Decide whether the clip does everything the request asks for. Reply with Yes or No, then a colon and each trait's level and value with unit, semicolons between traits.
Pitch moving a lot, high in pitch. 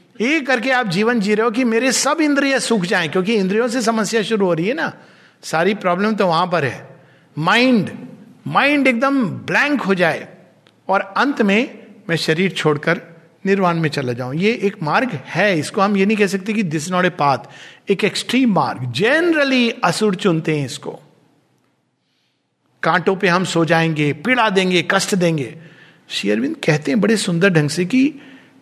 Yes: wide, 5.9 semitones; high, 195 Hz